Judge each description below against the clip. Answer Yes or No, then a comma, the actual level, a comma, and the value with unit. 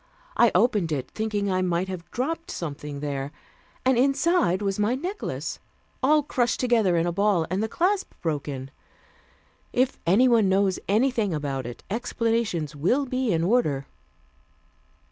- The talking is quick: No, average, 145 wpm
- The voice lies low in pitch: No, high, 200 Hz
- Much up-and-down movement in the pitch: Yes, wide, 6.9 semitones